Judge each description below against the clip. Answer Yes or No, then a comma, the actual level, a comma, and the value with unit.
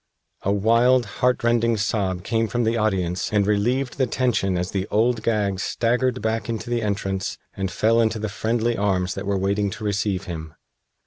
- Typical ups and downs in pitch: Yes, average, 3.0 semitones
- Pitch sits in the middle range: No, low, 110 Hz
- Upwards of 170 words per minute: Yes, average, 180 wpm